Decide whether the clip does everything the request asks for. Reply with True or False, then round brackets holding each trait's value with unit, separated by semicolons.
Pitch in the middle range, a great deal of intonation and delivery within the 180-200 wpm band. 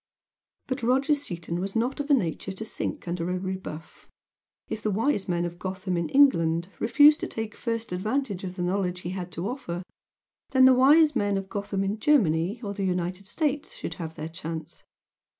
False (195 Hz; 5.9 semitones; 195 wpm)